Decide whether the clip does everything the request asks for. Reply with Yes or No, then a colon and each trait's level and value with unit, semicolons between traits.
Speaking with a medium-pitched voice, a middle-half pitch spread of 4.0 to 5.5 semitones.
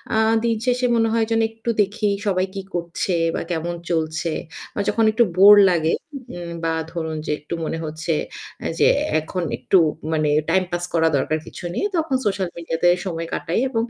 Yes: medium, 175 Hz; average, 4.8 semitones